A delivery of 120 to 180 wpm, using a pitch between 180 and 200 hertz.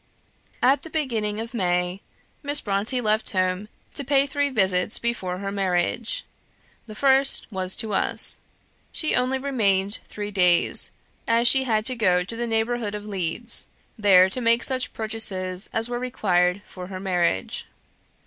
No: average, 155 wpm; high, 215 Hz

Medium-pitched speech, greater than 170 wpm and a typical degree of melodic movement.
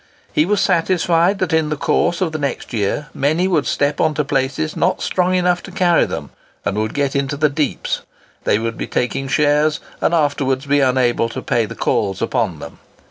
Yes: medium, 145 Hz; average, 200 wpm; average, 4.0 semitones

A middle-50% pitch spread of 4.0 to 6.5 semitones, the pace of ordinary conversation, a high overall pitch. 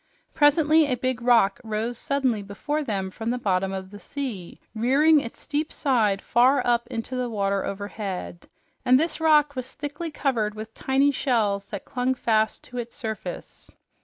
Yes: average, 4.9 semitones; average, 165 wpm; high, 240 Hz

